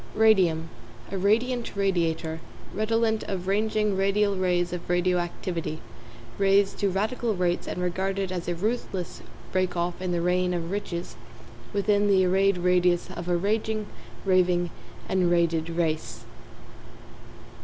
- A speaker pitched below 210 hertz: Yes, medium, 185 Hz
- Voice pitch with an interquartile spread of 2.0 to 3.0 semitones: Yes, narrow, 2.4 semitones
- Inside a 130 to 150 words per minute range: Yes, slow, 135 wpm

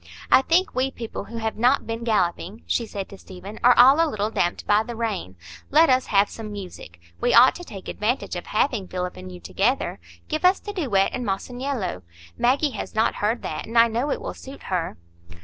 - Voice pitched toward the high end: Yes, high, 225 Hz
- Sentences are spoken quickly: Yes, fast, 215 wpm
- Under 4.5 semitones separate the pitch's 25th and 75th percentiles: No, average, 4.8 semitones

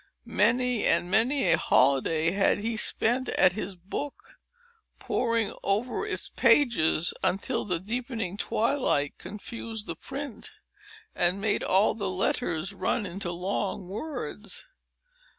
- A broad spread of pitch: No, average, 4.5 semitones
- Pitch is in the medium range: No, high, 205 Hz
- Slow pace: Yes, slow, 120 wpm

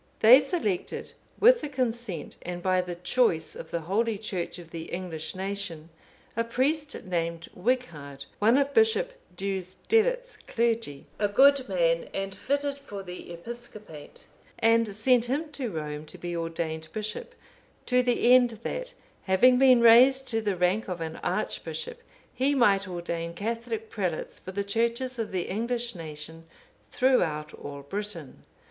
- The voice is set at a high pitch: Yes, high, 210 Hz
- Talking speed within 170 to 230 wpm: No, average, 150 wpm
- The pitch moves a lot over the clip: Yes, wide, 6.4 semitones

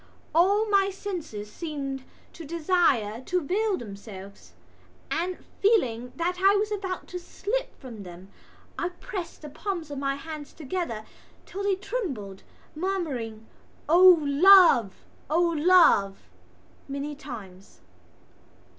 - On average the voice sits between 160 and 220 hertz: No, very high, 320 Hz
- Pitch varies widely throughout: Yes, wide, 7.5 semitones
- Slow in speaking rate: Yes, slow, 120 wpm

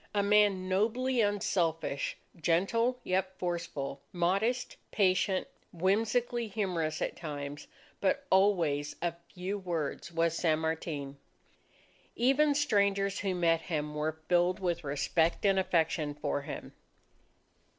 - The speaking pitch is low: No, medium, 180 Hz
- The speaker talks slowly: Yes, slow, 115 wpm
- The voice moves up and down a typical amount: Yes, average, 4.0 semitones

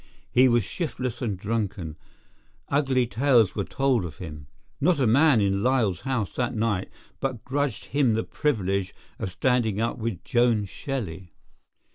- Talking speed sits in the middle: Yes, average, 150 wpm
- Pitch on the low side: Yes, low, 115 Hz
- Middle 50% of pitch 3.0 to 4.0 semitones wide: No, average, 4.9 semitones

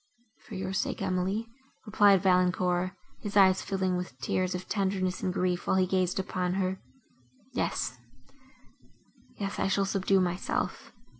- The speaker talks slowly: Yes, slow, 130 wpm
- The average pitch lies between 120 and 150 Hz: No, medium, 185 Hz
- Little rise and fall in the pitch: Yes, narrow, 1.3 semitones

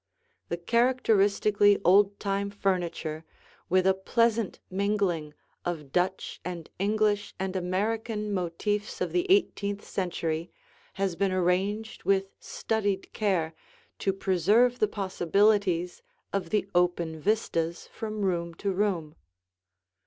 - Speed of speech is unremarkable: No, slow, 115 wpm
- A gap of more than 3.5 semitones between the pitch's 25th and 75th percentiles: No, average, 2.8 semitones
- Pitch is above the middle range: Yes, high, 195 Hz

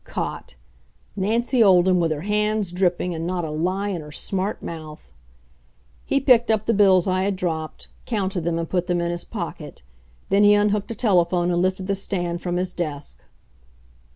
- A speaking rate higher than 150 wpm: Yes, average, 180 wpm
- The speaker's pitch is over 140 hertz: Yes, medium, 185 Hz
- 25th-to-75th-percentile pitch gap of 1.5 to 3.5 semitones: Yes, average, 2.9 semitones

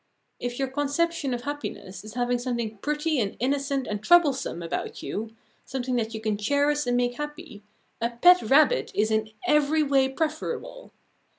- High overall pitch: Yes, very high, 265 Hz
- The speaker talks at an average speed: Yes, average, 165 wpm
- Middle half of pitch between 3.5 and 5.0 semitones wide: Yes, average, 4.5 semitones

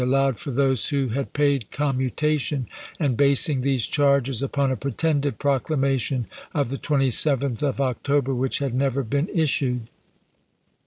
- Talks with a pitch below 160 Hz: Yes, low, 135 Hz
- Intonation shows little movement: Yes, narrow, 1.8 semitones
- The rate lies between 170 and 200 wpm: No, average, 145 wpm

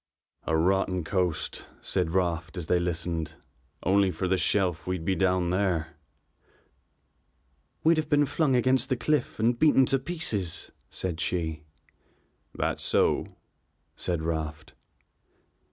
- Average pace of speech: No, slow, 125 wpm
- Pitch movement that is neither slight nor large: No, wide, 6.3 semitones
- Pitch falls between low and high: No, very low, 90 Hz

